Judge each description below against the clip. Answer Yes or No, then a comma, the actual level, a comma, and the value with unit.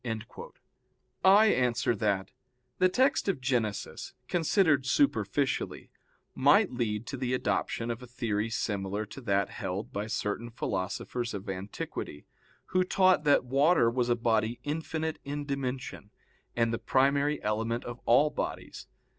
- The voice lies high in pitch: No, low, 120 Hz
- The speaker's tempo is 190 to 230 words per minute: No, slow, 135 wpm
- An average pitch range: Yes, average, 4.8 semitones